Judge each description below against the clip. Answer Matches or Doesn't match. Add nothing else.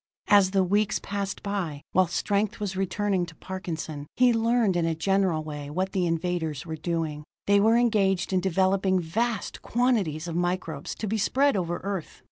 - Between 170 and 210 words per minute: Matches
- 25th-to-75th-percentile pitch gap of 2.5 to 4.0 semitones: Matches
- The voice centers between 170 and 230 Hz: Matches